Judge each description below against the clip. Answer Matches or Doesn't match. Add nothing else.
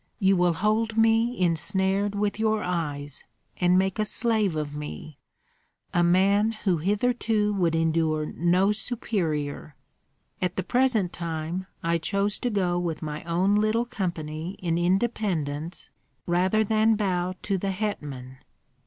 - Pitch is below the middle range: Doesn't match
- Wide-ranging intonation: Doesn't match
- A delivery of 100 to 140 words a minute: Matches